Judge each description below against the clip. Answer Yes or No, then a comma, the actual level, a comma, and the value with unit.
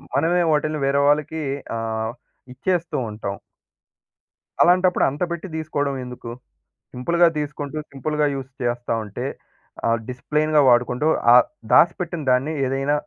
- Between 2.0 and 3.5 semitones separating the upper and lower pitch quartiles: No, average, 4.0 semitones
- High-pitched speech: No, medium, 145 Hz